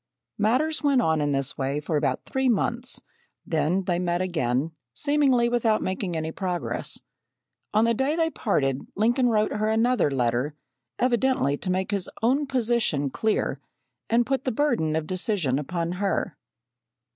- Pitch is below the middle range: No, high, 200 Hz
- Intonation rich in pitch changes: Yes, wide, 7.4 semitones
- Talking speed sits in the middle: Yes, average, 155 wpm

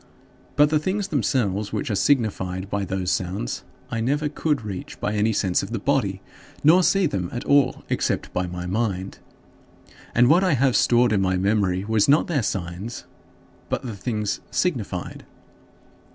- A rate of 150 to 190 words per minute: Yes, average, 165 wpm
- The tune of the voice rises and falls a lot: Yes, wide, 6.4 semitones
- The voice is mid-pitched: No, low, 110 Hz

